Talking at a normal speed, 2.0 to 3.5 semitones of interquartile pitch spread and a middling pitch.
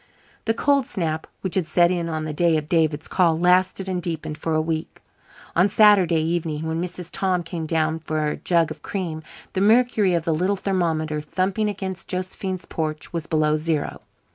Yes: average, 190 wpm; average, 2.9 semitones; medium, 170 Hz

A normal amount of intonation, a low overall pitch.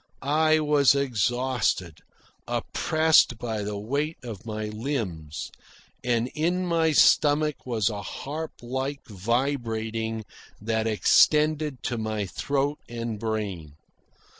Yes: average, 5.0 semitones; low, 120 Hz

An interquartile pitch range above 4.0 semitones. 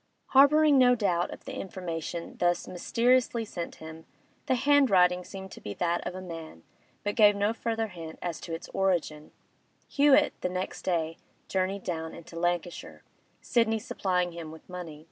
Yes: average, 4.9 semitones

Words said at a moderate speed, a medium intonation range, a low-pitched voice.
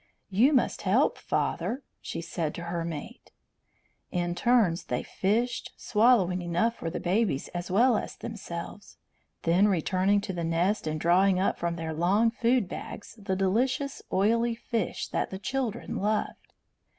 No: average, 150 wpm; average, 4.9 semitones; high, 195 Hz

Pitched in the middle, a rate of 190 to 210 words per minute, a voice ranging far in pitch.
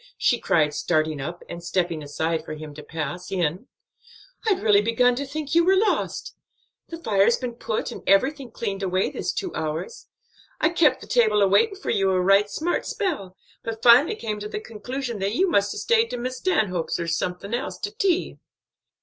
No: high, 215 Hz; average, 195 wpm; wide, 7.8 semitones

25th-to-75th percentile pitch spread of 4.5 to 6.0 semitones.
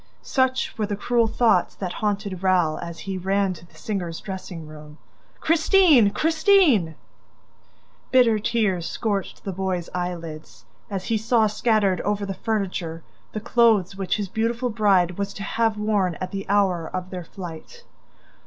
No: average, 3.7 semitones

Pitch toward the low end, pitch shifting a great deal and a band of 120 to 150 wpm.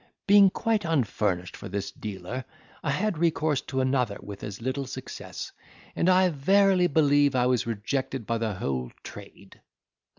Yes: low, 130 Hz; wide, 7.0 semitones; average, 145 wpm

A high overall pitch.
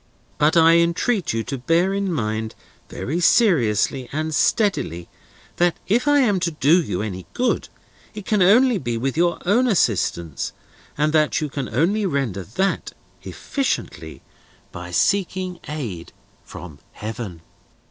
No: medium, 160 Hz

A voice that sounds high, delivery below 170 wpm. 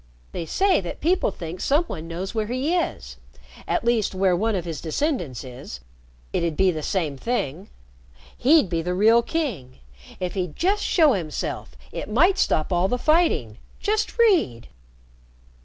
Yes: high, 195 Hz; average, 160 wpm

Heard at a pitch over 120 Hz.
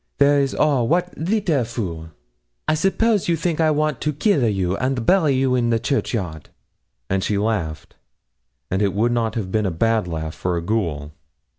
No: low, 115 Hz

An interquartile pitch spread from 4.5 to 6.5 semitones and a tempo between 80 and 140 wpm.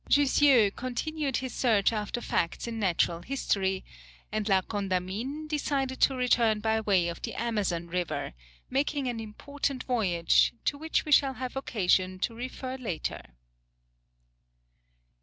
Yes: wide, 5.5 semitones; slow, 135 wpm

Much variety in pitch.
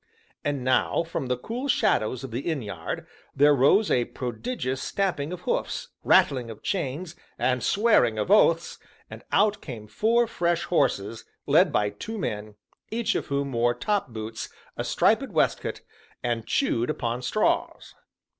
Yes: wide, 8.0 semitones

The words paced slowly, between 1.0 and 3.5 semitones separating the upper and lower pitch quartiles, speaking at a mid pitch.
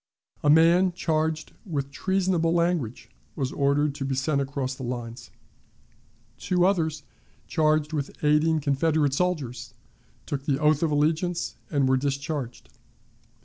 Yes: slow, 130 wpm; average, 3.0 semitones; medium, 150 Hz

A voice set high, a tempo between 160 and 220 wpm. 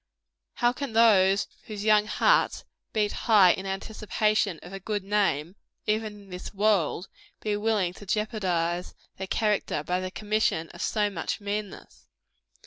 No: high, 205 Hz; average, 145 wpm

